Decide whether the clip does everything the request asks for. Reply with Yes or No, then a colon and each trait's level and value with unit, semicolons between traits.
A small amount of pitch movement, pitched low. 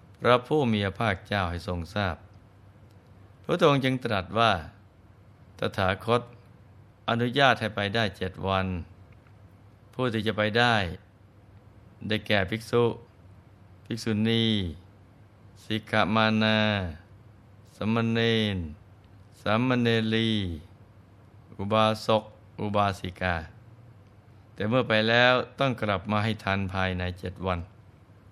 Yes: narrow, 2.2 semitones; low, 105 Hz